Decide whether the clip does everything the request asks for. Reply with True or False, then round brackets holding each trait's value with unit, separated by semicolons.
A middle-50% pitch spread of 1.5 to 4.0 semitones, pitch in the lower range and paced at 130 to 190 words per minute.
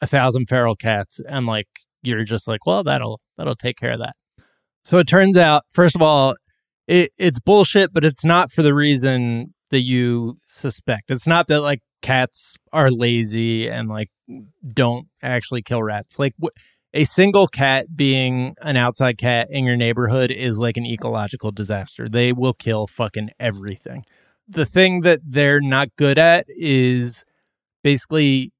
False (4.4 semitones; 130 Hz; 165 wpm)